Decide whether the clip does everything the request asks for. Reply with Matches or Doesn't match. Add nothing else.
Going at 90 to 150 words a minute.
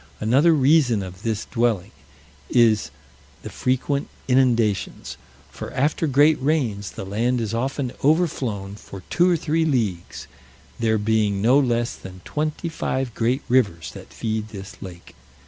Matches